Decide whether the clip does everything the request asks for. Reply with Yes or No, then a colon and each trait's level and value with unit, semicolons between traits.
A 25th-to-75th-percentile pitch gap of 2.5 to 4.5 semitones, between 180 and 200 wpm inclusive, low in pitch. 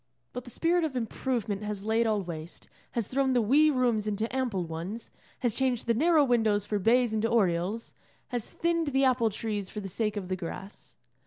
No: average, 3.7 semitones; average, 195 wpm; high, 225 Hz